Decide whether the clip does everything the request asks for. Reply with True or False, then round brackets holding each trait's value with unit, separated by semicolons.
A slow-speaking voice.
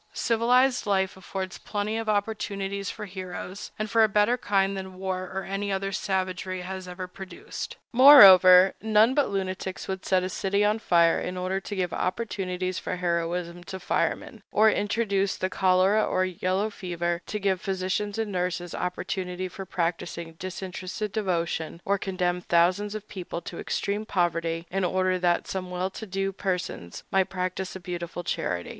False (165 wpm)